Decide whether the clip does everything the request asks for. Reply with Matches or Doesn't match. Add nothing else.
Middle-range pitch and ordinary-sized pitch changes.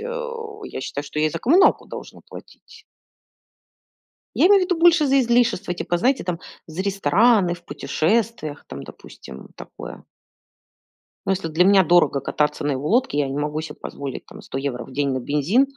Doesn't match